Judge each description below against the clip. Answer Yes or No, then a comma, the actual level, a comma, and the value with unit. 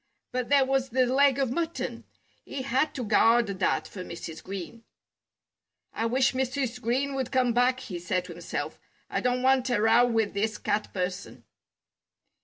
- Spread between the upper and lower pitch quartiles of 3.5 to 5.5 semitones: Yes, average, 3.9 semitones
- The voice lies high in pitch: Yes, high, 245 Hz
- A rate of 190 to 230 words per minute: No, average, 170 wpm